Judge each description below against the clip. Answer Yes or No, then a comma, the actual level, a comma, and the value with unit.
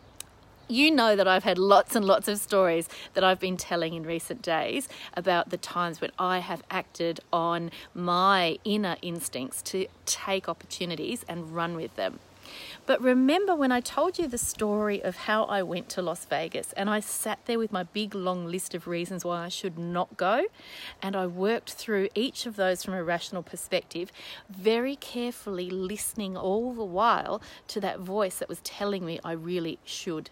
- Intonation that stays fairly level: No, average, 3.5 semitones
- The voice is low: No, medium, 185 Hz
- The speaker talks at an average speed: Yes, average, 185 wpm